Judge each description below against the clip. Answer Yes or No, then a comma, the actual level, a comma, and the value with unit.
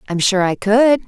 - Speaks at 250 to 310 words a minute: No, fast, 225 wpm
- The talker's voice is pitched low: No, high, 215 Hz